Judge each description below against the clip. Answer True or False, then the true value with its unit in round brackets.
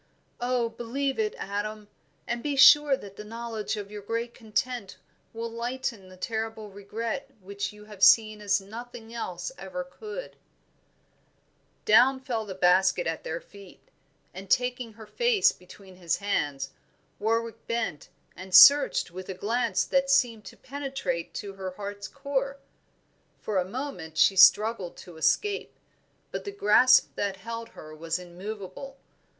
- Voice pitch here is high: True (215 Hz)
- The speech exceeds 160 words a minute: False (150 wpm)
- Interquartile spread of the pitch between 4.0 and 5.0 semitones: True (4.5 semitones)